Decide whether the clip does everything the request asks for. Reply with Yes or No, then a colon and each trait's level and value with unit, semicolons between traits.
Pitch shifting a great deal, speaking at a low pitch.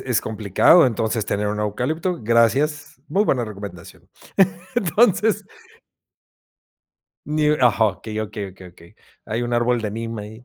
Yes: wide, 6.0 semitones; low, 115 Hz